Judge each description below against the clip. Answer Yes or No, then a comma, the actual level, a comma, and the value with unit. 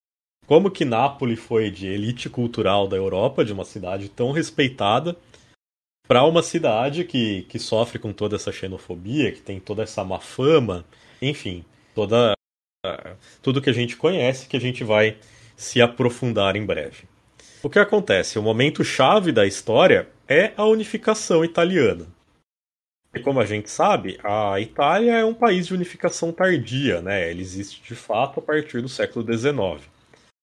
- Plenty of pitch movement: Yes, wide, 7.4 semitones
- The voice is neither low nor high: No, low, 120 Hz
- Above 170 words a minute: No, average, 160 wpm